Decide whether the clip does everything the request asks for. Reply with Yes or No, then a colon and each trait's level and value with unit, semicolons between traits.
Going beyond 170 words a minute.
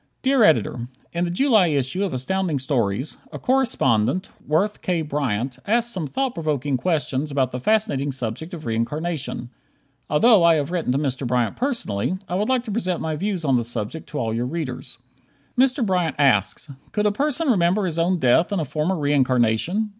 Yes: average, 185 wpm